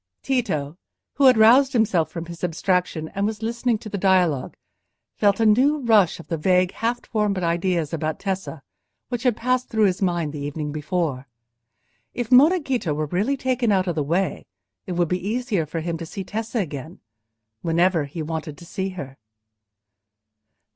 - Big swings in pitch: Yes, wide, 5.7 semitones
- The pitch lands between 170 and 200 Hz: Yes, medium, 185 Hz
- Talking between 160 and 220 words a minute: Yes, average, 175 wpm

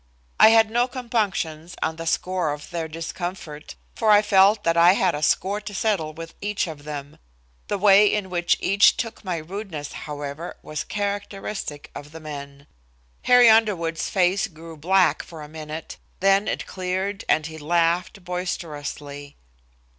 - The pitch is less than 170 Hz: No, medium, 175 Hz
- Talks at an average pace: Yes, average, 160 wpm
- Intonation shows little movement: No, average, 4.5 semitones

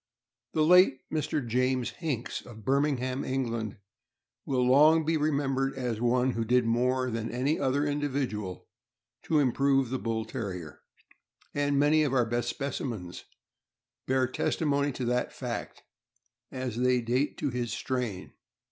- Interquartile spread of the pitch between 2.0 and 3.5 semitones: Yes, average, 2.9 semitones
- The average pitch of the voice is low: Yes, low, 130 Hz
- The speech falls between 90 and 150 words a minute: Yes, average, 140 wpm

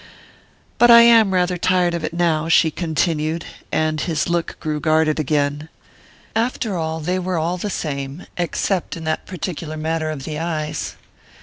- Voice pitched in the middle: Yes, medium, 165 Hz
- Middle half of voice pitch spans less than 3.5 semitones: Yes, narrow, 2.5 semitones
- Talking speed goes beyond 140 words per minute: Yes, average, 165 wpm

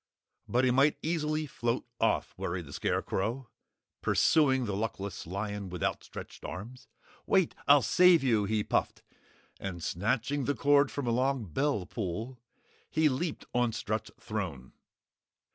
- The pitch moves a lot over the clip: Yes, wide, 6.0 semitones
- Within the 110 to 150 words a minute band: Yes, average, 140 wpm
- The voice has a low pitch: Yes, low, 120 Hz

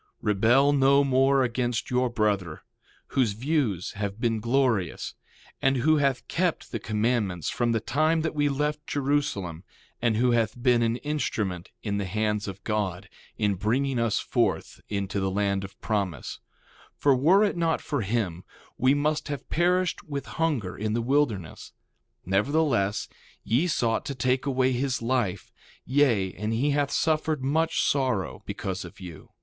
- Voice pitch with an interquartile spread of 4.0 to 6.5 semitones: Yes, wide, 5.6 semitones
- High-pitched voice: No, low, 120 Hz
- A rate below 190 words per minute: Yes, average, 160 wpm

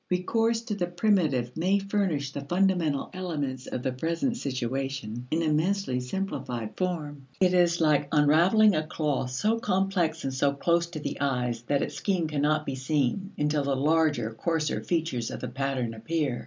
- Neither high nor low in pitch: Yes, medium, 155 Hz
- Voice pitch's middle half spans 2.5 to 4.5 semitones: No, average, 5.1 semitones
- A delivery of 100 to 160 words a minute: No, average, 170 wpm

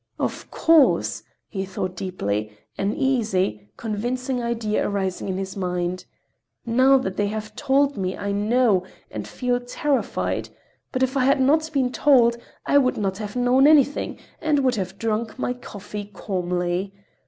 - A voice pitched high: Yes, high, 220 Hz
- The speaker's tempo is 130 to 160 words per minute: Yes, average, 155 wpm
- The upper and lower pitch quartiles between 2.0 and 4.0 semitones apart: No, average, 5.2 semitones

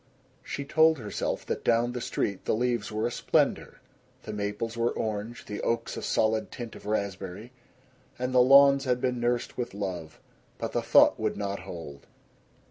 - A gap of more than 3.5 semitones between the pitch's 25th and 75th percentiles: No, average, 3.2 semitones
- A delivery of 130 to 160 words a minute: No, average, 175 wpm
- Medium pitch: No, low, 115 Hz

